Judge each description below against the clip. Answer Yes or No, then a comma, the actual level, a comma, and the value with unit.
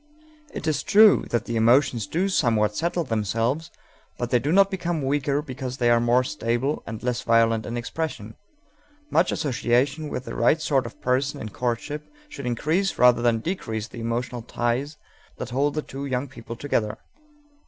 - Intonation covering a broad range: No, average, 4.0 semitones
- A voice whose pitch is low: Yes, low, 125 Hz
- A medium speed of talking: Yes, average, 175 wpm